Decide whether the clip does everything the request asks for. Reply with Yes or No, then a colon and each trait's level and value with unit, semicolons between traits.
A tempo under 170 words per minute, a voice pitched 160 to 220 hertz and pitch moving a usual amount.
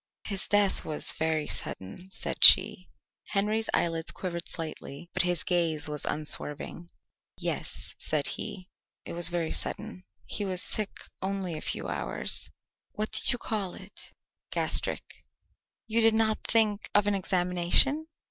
Yes: average, 140 wpm; medium, 185 Hz; average, 3.8 semitones